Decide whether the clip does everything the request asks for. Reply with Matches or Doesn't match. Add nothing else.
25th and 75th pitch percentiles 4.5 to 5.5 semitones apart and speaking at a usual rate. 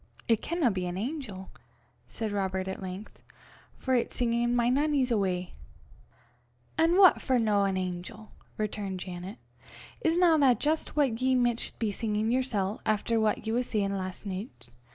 Matches